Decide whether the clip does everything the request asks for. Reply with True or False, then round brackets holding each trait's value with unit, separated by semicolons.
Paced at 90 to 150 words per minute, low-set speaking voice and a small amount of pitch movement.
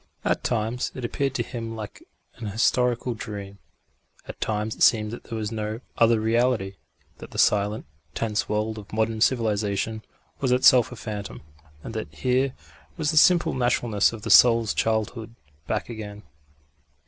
False (160 wpm; 110 Hz; 2.3 semitones)